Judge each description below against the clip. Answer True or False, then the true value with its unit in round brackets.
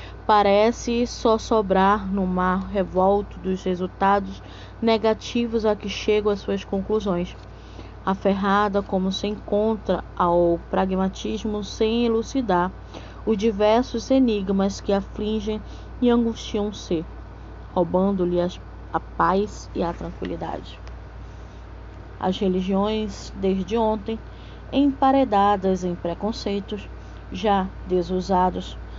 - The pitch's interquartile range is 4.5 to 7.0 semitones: False (2.9 semitones)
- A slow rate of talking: True (95 wpm)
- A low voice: False (200 Hz)